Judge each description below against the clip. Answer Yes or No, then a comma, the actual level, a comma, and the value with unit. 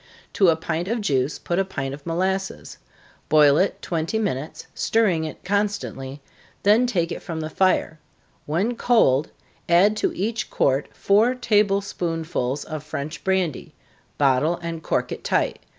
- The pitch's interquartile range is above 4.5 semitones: Yes, average, 4.9 semitones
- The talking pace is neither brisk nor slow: Yes, average, 150 wpm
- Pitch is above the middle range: No, medium, 170 Hz